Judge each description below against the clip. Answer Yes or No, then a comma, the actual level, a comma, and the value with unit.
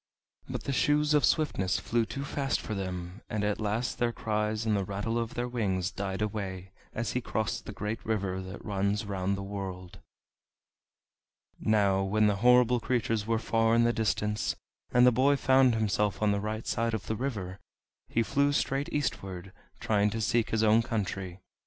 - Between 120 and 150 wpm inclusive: No, average, 185 wpm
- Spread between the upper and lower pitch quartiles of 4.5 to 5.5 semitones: No, average, 3.1 semitones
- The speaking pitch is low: Yes, low, 110 Hz